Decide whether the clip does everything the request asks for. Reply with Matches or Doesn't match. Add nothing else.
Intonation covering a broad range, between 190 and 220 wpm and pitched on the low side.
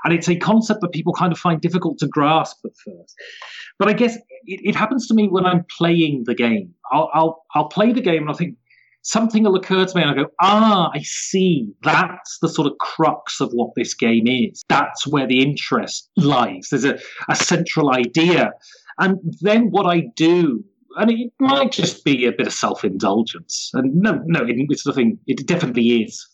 Doesn't match